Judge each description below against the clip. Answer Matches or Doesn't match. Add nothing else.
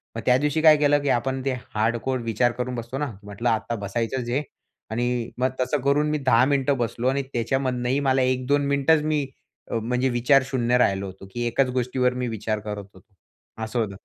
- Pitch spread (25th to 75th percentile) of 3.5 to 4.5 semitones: Doesn't match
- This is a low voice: Matches